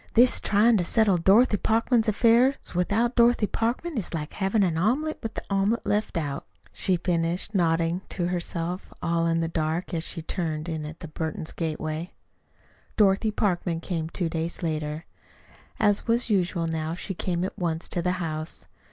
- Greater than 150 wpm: Yes, average, 165 wpm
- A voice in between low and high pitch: Yes, medium, 180 Hz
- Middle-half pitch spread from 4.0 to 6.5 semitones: Yes, average, 4.4 semitones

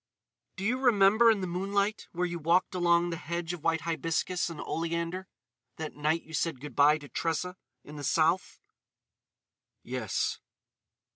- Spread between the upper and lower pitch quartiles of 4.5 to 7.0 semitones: No, average, 2.8 semitones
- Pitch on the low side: No, medium, 170 Hz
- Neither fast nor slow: Yes, average, 150 wpm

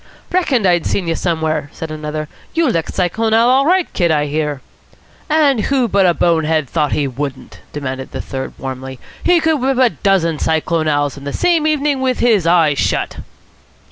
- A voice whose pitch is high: No, medium, 170 Hz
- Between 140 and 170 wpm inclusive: No, average, 190 wpm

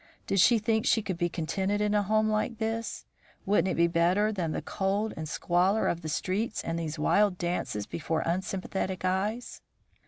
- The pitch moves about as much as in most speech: Yes, average, 3.7 semitones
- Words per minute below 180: No, average, 185 wpm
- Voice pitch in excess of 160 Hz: Yes, high, 190 Hz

